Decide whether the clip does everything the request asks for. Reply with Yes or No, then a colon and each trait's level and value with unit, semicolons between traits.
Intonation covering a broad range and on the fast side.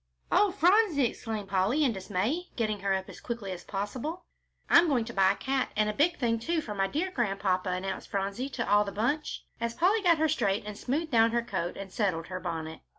Yes: wide, 7.1 semitones; fast, 220 wpm